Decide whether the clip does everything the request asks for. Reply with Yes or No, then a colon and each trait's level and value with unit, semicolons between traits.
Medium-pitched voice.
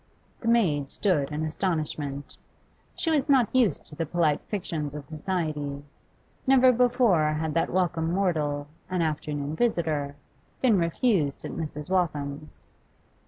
Yes: medium, 160 Hz